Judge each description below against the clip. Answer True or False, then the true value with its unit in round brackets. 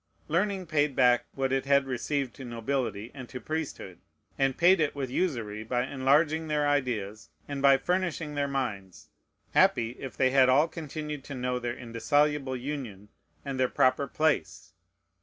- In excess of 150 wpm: True (160 wpm)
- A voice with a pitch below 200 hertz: True (135 Hz)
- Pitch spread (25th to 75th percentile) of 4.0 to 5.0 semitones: False (3.3 semitones)